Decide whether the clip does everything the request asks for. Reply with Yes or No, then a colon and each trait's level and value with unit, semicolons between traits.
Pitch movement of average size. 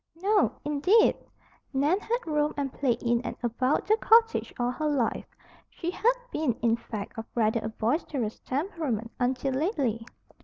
No: wide, 6.0 semitones